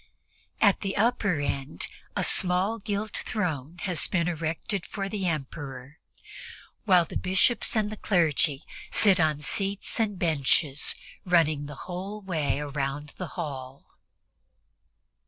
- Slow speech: Yes, slow, 125 wpm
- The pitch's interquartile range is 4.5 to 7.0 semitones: Yes, average, 5.1 semitones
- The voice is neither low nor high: Yes, medium, 175 Hz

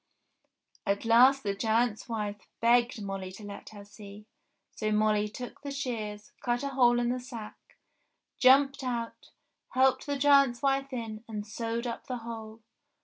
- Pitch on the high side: Yes, high, 230 Hz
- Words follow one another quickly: No, average, 160 wpm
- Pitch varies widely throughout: No, average, 3.2 semitones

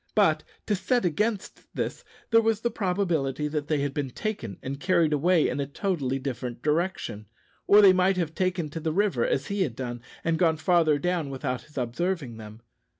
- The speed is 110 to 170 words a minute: No, average, 195 wpm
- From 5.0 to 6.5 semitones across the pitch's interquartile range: Yes, wide, 5.4 semitones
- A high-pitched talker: No, medium, 160 Hz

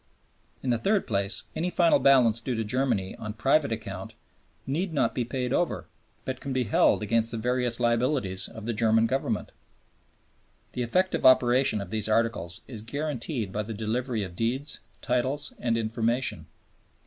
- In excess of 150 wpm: Yes, average, 160 wpm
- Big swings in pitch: No, average, 3.2 semitones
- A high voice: No, low, 120 Hz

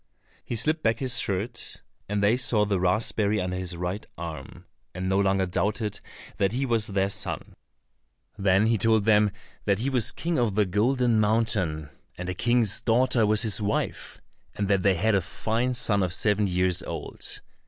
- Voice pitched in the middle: No, low, 105 Hz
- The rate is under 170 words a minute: No, average, 180 wpm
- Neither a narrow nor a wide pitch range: Yes, average, 3.1 semitones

